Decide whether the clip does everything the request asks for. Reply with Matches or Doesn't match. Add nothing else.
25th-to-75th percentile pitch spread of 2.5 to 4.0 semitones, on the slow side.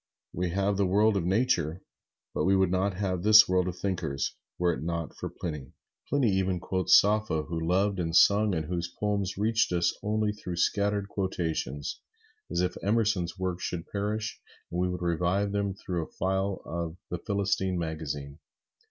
Doesn't match